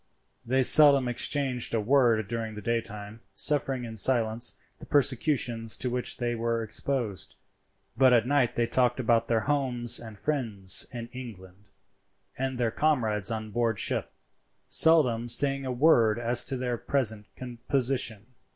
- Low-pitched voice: Yes, low, 120 Hz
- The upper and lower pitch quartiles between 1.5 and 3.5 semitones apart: Yes, average, 2.8 semitones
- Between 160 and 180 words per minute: No, average, 145 wpm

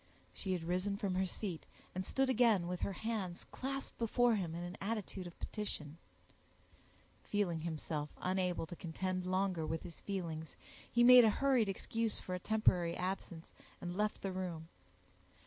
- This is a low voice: No, medium, 185 Hz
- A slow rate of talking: No, average, 165 wpm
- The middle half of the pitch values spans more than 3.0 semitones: Yes, average, 3.5 semitones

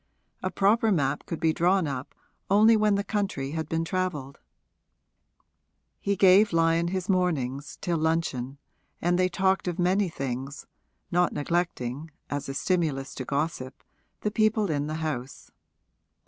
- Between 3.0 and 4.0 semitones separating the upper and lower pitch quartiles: No, average, 4.9 semitones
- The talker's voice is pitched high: No, medium, 165 Hz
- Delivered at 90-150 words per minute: Yes, average, 145 wpm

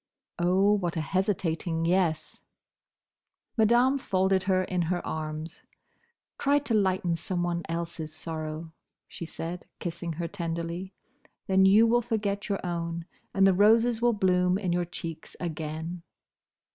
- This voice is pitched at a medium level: Yes, medium, 180 Hz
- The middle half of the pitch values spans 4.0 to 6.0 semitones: No, average, 3.0 semitones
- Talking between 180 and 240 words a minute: No, slow, 135 wpm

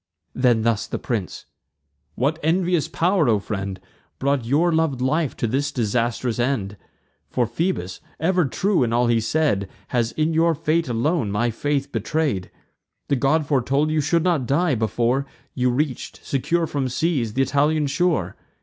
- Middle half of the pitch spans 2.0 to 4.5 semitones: No, average, 5.1 semitones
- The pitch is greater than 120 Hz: Yes, low, 135 Hz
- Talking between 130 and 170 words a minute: Yes, average, 160 wpm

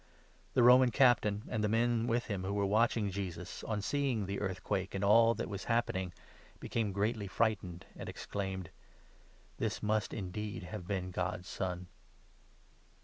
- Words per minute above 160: No, average, 155 wpm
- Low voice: Yes, low, 105 Hz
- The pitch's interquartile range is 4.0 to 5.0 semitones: No, average, 3.3 semitones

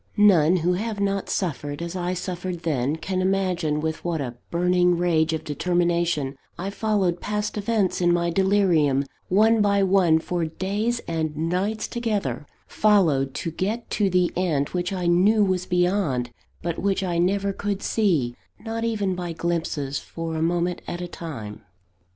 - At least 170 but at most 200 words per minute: No, average, 160 wpm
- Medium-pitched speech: Yes, medium, 180 Hz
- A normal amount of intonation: Yes, average, 3.4 semitones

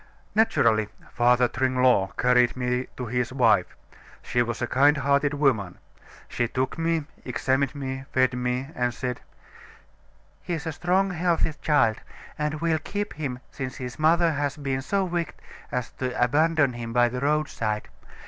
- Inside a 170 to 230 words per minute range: No, average, 150 wpm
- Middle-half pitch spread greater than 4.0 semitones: No, average, 3.7 semitones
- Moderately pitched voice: No, low, 130 Hz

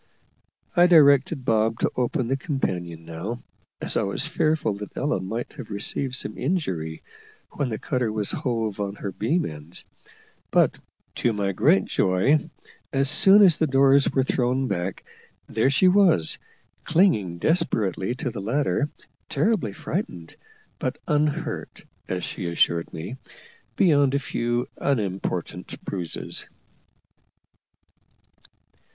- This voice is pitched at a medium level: No, low, 120 Hz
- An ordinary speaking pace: No, slow, 130 wpm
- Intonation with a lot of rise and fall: Yes, wide, 6.7 semitones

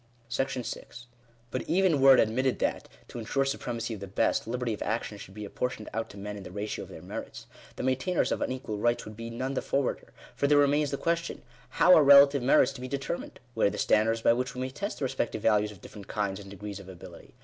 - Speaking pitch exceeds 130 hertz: No, low, 120 Hz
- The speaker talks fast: Yes, fast, 240 wpm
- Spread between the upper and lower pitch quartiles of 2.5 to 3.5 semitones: No, average, 4.4 semitones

